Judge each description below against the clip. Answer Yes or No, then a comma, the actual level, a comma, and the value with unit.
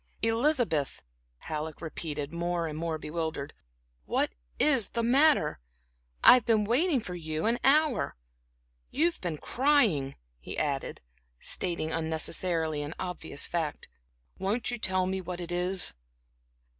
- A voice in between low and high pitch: Yes, medium, 175 Hz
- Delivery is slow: Yes, slow, 125 wpm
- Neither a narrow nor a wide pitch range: No, wide, 6.8 semitones